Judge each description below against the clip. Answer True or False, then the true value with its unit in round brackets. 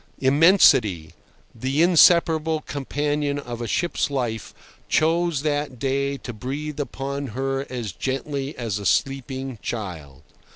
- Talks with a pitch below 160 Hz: True (135 Hz)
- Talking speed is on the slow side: True (120 wpm)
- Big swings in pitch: False (3.5 semitones)